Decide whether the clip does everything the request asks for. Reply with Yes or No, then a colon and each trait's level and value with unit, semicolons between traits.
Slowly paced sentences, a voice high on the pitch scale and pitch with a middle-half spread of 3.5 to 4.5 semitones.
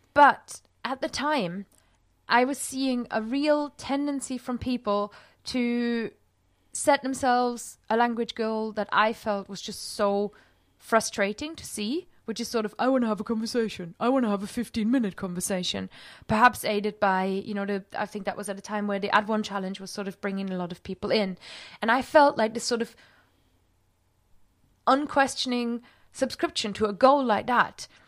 No: average, 185 wpm; high, 220 Hz; average, 3.8 semitones